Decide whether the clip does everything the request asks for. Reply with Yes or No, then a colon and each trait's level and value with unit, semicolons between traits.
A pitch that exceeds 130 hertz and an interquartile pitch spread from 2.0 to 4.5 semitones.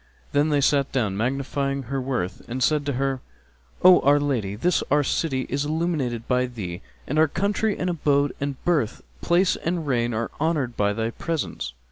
Yes: medium, 140 Hz; average, 4.1 semitones